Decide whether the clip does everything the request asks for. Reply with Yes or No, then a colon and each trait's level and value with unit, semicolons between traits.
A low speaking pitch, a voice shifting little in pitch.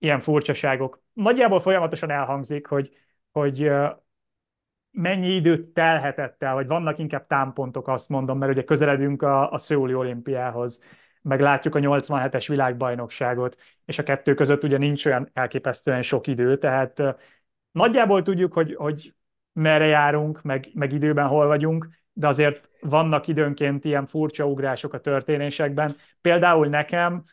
No: medium, 145 Hz; narrow, 2.1 semitones